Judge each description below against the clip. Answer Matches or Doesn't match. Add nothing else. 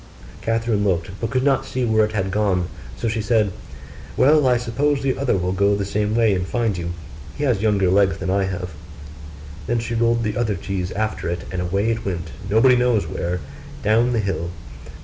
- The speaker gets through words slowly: Doesn't match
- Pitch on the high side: Doesn't match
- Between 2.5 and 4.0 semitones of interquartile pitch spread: Matches